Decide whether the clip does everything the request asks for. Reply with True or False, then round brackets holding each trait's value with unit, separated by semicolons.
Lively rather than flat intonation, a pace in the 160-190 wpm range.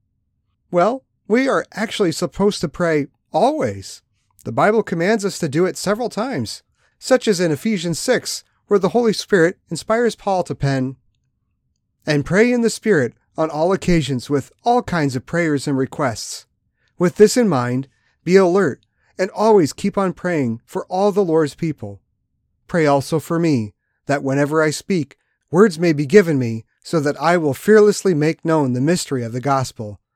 True (6.4 semitones; 170 wpm)